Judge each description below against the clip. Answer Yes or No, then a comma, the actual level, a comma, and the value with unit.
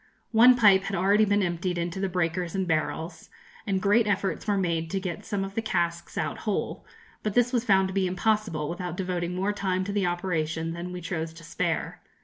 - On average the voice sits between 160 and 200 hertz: Yes, medium, 185 Hz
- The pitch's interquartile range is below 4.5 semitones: Yes, average, 2.8 semitones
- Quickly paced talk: Yes, fast, 210 wpm